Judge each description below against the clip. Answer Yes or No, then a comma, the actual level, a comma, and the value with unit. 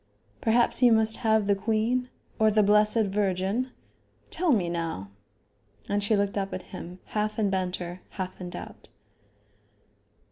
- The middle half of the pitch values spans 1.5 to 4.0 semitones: Yes, average, 2.9 semitones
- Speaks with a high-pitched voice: Yes, high, 205 Hz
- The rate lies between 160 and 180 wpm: No, average, 145 wpm